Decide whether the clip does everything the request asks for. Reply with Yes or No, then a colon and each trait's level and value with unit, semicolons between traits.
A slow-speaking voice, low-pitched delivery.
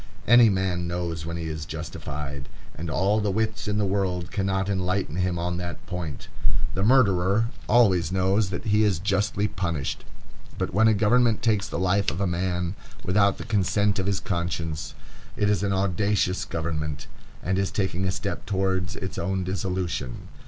No: average, 175 wpm; very low, 95 Hz